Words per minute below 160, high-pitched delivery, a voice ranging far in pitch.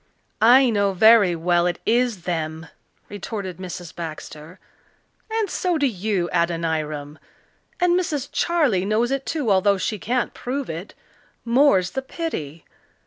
Yes: slow, 135 wpm; high, 200 Hz; wide, 6.8 semitones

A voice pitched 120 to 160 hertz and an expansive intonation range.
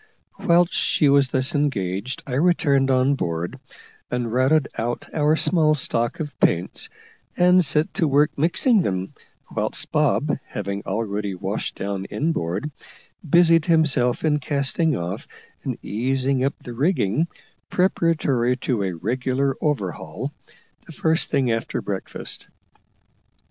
Yes: low, 135 Hz; wide, 5.9 semitones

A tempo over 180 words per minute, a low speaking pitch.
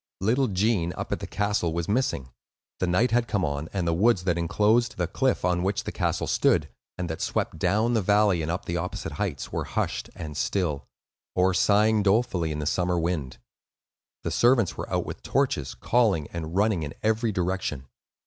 Yes: average, 195 wpm; very low, 95 Hz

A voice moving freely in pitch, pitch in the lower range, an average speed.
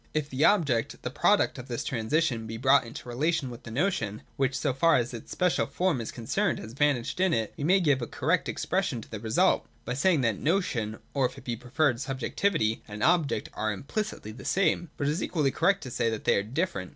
No: wide, 6.0 semitones; low, 130 Hz; fast, 230 wpm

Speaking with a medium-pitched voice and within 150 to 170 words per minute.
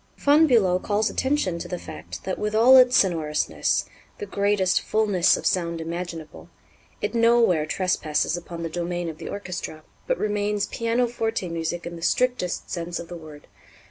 Yes: medium, 180 Hz; average, 165 wpm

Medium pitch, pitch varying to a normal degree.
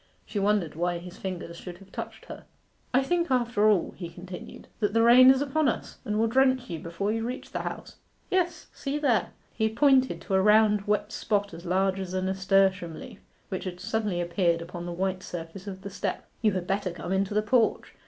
No: high, 200 Hz; average, 4.0 semitones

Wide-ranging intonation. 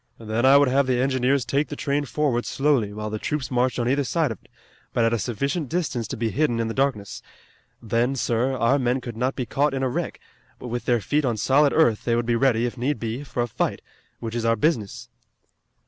No: average, 3.1 semitones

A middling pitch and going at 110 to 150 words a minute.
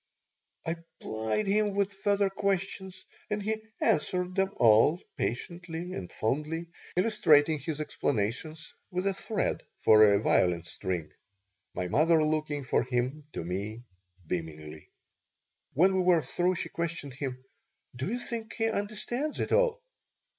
Yes: medium, 160 Hz; slow, 135 wpm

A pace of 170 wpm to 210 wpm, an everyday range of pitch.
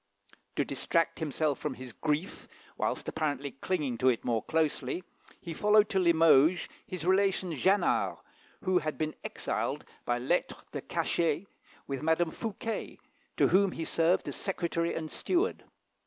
No: average, 145 wpm; average, 3.9 semitones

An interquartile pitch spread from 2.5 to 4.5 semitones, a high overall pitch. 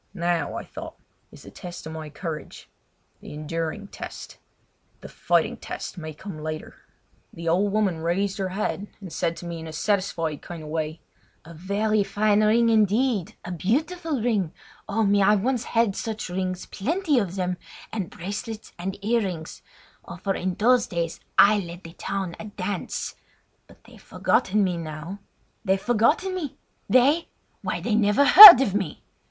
Yes: average, 4.2 semitones; high, 195 Hz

